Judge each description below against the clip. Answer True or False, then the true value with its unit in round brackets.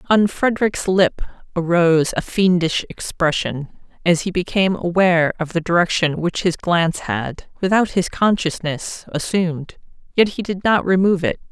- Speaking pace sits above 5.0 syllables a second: False (4.9 syllables/s)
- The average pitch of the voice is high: False (175 Hz)